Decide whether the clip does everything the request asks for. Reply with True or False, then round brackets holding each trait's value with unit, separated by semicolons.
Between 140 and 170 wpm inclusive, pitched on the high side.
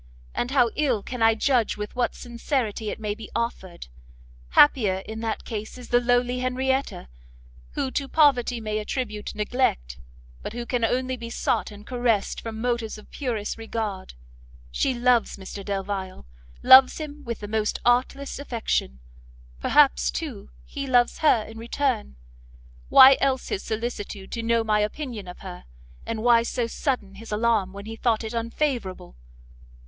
True (160 wpm; 230 Hz)